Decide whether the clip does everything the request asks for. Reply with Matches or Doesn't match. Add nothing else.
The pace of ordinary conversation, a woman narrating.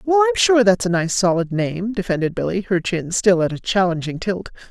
Doesn't match